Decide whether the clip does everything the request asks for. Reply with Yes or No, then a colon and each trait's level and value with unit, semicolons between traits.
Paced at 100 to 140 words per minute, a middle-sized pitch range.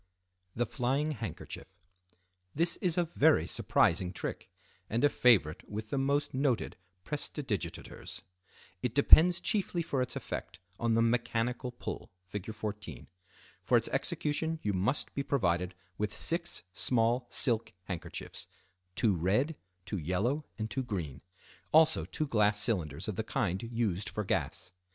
No: slow, 135 wpm; wide, 6.7 semitones